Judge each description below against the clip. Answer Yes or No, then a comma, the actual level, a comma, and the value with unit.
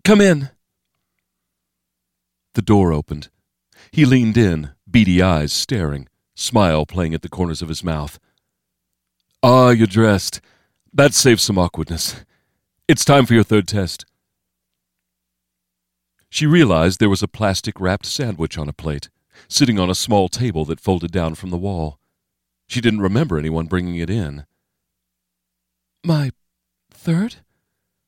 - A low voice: Yes, very low, 90 Hz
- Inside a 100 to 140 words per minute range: Yes, slow, 135 wpm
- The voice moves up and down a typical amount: No, wide, 7.3 semitones